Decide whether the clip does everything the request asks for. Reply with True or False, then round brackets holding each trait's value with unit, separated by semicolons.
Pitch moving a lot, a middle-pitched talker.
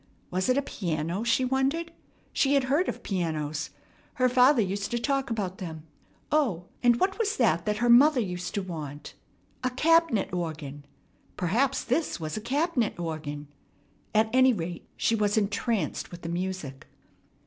False (7.2 semitones; 210 Hz)